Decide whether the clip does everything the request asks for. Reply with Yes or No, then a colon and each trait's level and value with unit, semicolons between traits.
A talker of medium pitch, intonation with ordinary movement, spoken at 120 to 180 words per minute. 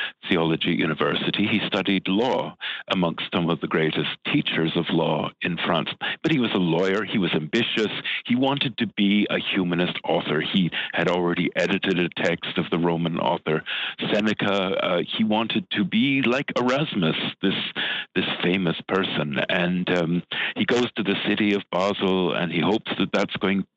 No: very low, 95 Hz; average, 3.3 semitones; average, 170 wpm